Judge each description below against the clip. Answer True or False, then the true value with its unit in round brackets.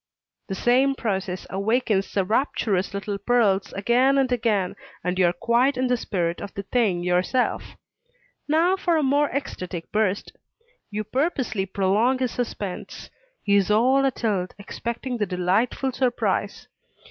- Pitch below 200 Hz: False (220 Hz)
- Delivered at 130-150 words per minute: True (145 wpm)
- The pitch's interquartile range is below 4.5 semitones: False (4.8 semitones)